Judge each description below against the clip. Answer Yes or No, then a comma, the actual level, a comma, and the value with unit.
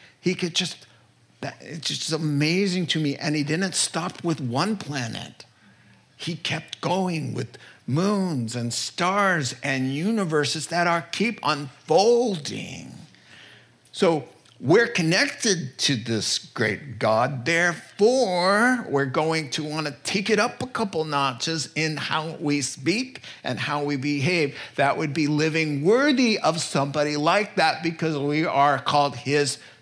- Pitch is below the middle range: No, medium, 155 Hz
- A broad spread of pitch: No, average, 4.1 semitones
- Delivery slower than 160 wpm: Yes, average, 140 wpm